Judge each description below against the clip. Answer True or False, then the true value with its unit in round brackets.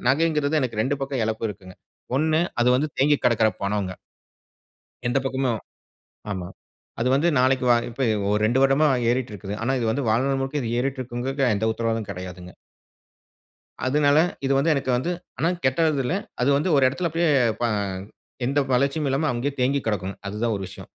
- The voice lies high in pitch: False (130 Hz)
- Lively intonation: False (4.0 semitones)